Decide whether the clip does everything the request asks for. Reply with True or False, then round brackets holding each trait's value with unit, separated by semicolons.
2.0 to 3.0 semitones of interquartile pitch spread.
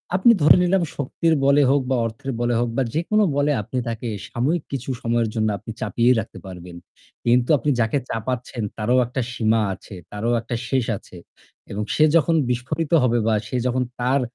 False (3.7 semitones)